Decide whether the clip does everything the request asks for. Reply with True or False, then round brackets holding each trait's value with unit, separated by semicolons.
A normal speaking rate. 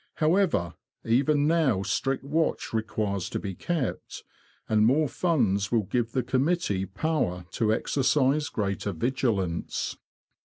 False (120 wpm)